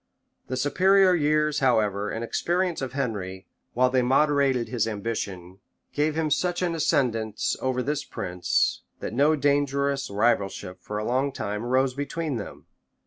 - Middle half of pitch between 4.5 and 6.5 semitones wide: Yes, average, 5.1 semitones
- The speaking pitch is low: Yes, low, 130 Hz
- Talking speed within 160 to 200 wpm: No, average, 145 wpm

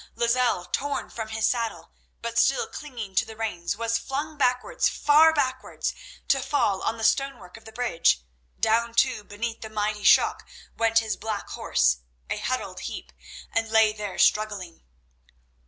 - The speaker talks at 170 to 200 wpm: No, average, 155 wpm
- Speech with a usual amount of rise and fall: Yes, average, 3.0 semitones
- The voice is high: Yes, high, 225 Hz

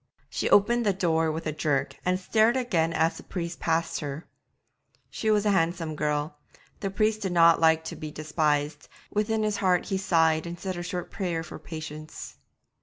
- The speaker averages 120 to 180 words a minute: No, average, 190 wpm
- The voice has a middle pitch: Yes, medium, 170 Hz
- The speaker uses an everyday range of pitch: Yes, average, 3.8 semitones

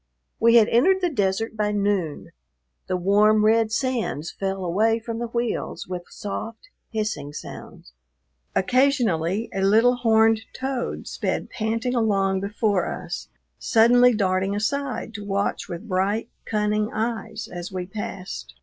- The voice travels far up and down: No, average, 3.0 semitones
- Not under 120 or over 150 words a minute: Yes, slow, 135 wpm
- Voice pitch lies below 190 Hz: No, high, 215 Hz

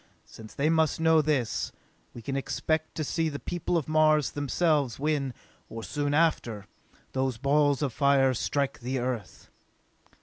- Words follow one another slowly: No, average, 155 wpm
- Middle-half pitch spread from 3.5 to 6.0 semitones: No, average, 3.1 semitones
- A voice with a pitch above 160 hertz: No, medium, 145 Hz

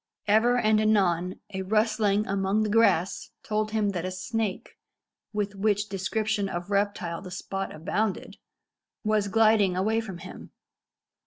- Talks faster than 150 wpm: No, average, 140 wpm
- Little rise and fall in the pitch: Yes, narrow, 2.2 semitones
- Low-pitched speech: No, high, 205 Hz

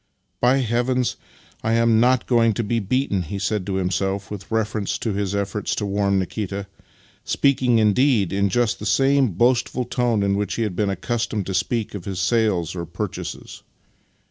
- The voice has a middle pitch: No, low, 105 Hz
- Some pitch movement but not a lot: Yes, average, 3.4 semitones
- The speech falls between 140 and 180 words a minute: No, average, 190 wpm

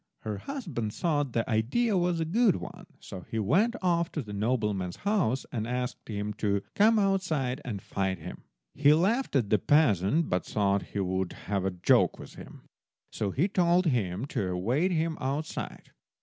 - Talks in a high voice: No, low, 130 Hz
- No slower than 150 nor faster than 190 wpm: Yes, average, 180 wpm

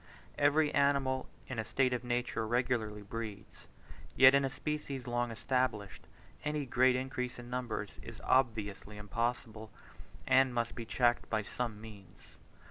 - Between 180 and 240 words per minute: No, average, 140 wpm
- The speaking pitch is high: No, low, 120 Hz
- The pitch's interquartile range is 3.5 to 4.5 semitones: No, average, 3.0 semitones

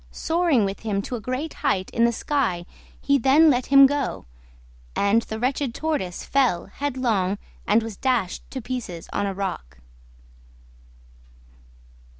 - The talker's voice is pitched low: No, high, 240 Hz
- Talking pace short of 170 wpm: Yes, average, 145 wpm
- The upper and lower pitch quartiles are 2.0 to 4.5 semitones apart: No, wide, 5.6 semitones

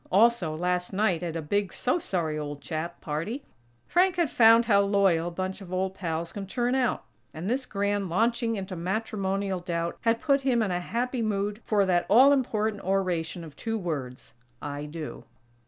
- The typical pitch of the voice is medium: No, high, 195 Hz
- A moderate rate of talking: Yes, average, 185 wpm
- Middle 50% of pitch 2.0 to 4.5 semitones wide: No, average, 4.9 semitones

